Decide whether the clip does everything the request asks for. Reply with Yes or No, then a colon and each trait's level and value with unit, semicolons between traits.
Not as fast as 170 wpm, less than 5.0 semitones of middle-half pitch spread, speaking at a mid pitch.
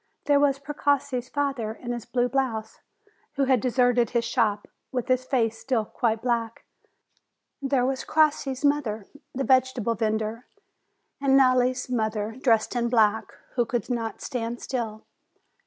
No: average, 140 wpm; average, 2.8 semitones; high, 245 Hz